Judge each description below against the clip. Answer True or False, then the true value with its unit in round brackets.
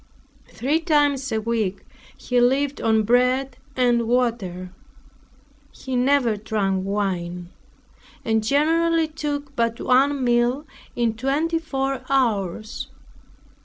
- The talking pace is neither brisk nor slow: False (105 wpm)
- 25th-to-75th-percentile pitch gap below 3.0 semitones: False (4.2 semitones)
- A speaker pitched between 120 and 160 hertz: False (245 Hz)